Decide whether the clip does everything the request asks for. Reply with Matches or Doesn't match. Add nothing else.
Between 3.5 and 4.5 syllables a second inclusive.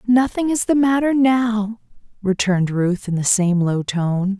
Matches